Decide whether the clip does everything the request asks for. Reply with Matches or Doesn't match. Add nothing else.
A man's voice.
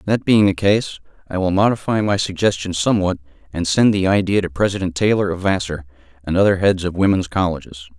Matches